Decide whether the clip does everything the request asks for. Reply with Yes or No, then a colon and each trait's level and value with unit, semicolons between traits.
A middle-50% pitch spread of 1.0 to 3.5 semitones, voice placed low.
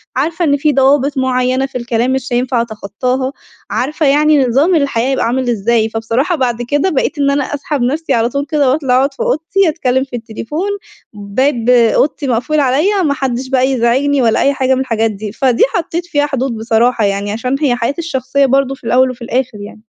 No: average, 3.2 semitones; very high, 260 Hz